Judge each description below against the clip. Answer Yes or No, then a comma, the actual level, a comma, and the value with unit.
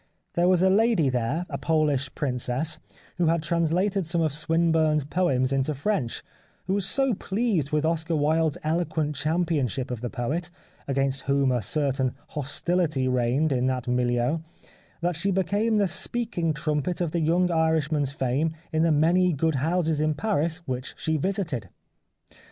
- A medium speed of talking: Yes, average, 155 wpm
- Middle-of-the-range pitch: Yes, medium, 155 Hz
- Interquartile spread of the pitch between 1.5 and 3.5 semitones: No, average, 4.0 semitones